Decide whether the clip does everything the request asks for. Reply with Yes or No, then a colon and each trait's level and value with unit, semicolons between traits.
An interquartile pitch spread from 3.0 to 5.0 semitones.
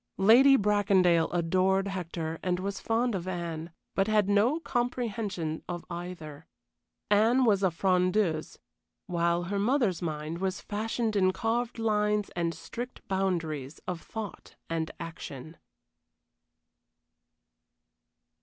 Yes: average, 4.0 semitones